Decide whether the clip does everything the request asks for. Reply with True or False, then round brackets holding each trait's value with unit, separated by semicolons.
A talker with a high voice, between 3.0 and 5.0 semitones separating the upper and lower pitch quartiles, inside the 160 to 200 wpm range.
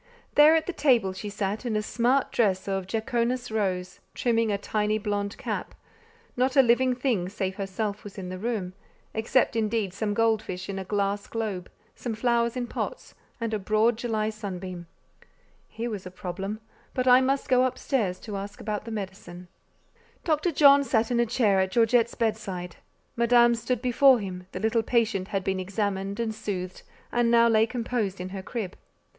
True (220 Hz; 3.5 semitones; 185 wpm)